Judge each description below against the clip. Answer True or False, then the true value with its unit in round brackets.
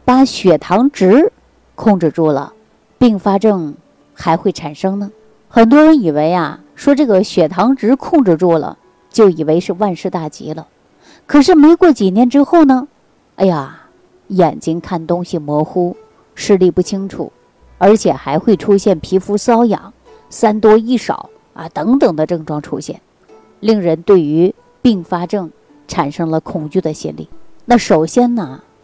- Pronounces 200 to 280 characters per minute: True (220 characters per minute)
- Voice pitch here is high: True (195 Hz)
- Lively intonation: True (6.4 semitones)